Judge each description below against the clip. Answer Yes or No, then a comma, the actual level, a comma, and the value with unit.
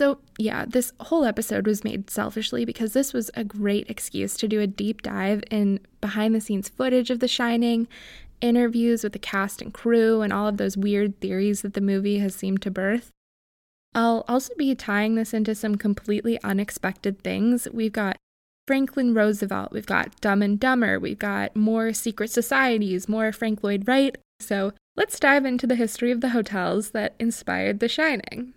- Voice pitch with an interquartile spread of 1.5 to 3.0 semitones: Yes, average, 2.7 semitones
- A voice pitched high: Yes, high, 220 Hz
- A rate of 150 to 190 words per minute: Yes, average, 185 wpm